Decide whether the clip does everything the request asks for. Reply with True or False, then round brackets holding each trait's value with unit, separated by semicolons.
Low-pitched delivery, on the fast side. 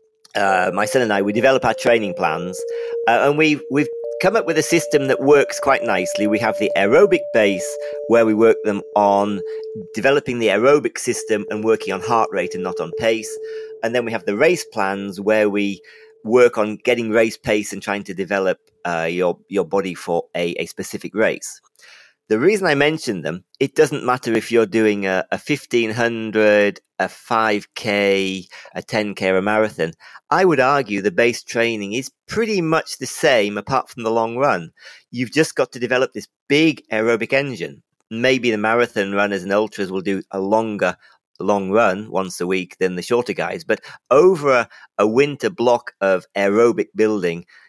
False (115 Hz; 185 wpm)